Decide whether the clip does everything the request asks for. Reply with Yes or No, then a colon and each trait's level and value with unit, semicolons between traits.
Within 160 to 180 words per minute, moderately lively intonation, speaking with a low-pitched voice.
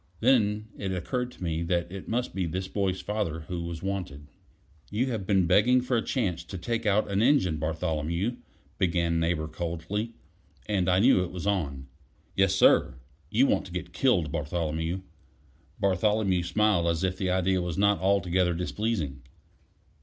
Yes: average, 165 wpm; average, 3.6 semitones; very low, 95 Hz